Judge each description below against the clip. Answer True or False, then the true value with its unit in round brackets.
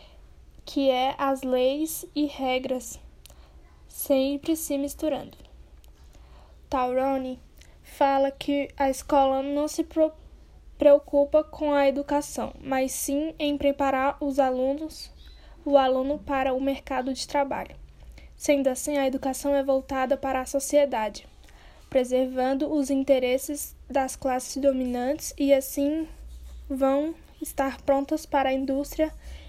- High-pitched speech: True (275 Hz)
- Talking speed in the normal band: False (115 wpm)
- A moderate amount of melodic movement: False (1.9 semitones)